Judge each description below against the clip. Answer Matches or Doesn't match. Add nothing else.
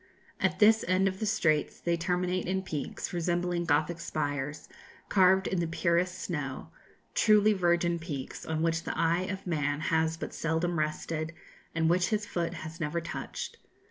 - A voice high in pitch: Doesn't match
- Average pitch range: Doesn't match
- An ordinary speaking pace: Matches